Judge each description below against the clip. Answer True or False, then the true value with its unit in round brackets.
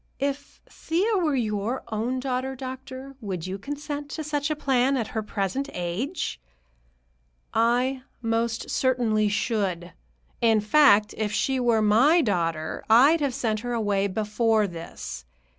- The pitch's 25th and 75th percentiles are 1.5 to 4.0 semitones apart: False (4.5 semitones)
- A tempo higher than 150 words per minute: False (140 wpm)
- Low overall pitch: False (235 Hz)